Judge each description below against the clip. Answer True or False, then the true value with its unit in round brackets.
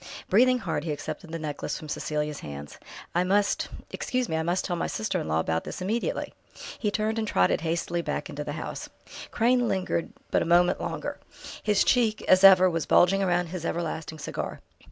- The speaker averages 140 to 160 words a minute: False (195 wpm)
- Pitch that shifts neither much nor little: True (4.6 semitones)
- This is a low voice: False (175 Hz)